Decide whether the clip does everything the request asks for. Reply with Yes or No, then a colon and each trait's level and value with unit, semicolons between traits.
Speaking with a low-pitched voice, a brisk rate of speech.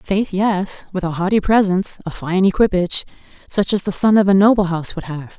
No: high, 190 Hz; fast, 210 wpm